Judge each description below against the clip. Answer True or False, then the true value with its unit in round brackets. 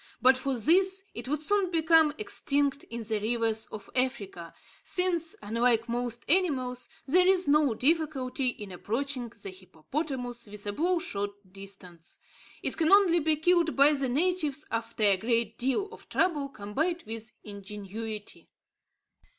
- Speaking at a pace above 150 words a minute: False (140 wpm)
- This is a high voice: True (255 Hz)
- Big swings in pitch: True (6.5 semitones)